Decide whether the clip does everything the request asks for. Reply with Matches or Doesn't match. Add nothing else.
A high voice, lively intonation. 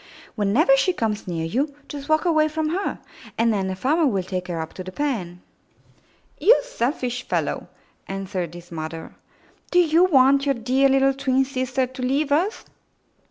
Matches